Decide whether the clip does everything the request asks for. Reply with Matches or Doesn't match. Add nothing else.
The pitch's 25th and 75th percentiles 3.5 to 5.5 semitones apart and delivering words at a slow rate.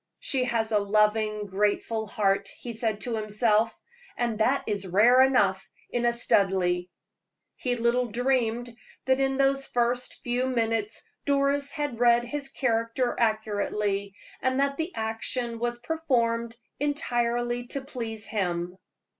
Doesn't match